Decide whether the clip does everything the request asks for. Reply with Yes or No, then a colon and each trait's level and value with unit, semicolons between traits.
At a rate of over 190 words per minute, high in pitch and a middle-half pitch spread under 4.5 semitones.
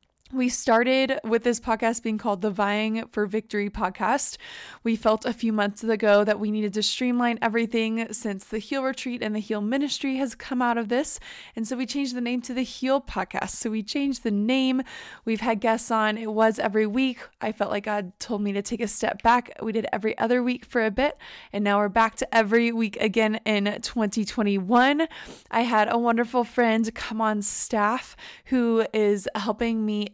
Yes: average, 200 wpm; high, 225 Hz; narrow, 2.6 semitones